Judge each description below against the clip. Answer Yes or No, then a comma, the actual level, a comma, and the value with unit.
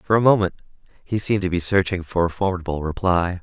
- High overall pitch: No, very low, 90 Hz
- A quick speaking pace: Yes, fast, 210 wpm